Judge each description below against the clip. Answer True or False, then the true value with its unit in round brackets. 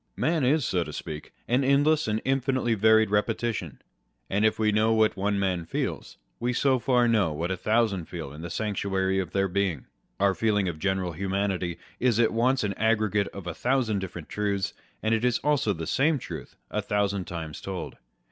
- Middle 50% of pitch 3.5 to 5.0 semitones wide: True (3.8 semitones)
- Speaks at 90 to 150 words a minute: False (195 wpm)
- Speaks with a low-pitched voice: True (105 Hz)